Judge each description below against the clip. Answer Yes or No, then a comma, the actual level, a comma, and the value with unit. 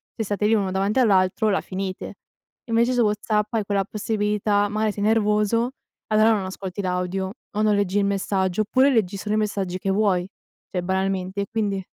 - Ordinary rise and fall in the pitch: No, narrow, 2.1 semitones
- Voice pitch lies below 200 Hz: No, high, 205 Hz